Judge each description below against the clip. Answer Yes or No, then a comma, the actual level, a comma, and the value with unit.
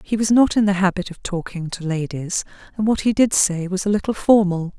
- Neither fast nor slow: No, fast, 240 wpm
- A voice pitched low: No, high, 190 Hz